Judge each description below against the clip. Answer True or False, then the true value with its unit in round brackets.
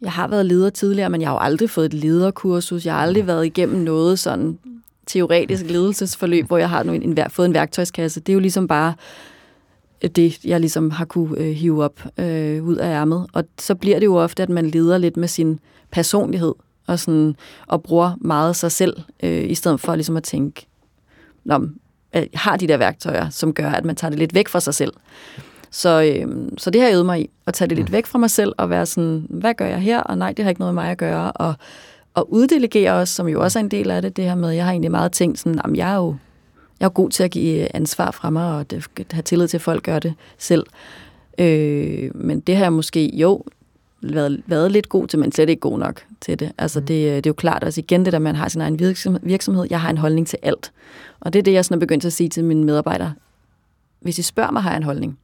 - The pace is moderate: False (250 wpm)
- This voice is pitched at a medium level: True (170 Hz)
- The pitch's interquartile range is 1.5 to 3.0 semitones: True (2.5 semitones)